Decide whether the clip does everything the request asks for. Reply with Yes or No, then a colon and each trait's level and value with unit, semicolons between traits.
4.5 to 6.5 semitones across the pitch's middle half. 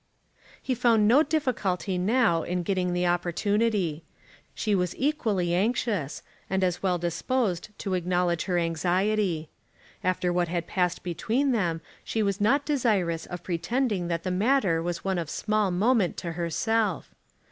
No: average, 4.1 semitones